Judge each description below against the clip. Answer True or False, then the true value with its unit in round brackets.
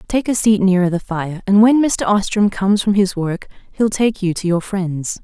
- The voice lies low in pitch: False (195 Hz)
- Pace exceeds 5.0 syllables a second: False (4.8 syllables/s)